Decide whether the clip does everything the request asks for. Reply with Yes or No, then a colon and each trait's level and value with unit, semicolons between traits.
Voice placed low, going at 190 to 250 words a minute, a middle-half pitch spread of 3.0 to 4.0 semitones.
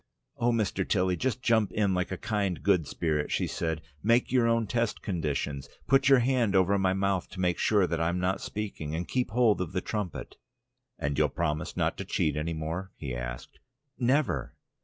No: very low, 95 Hz; average, 195 wpm; wide, 5.4 semitones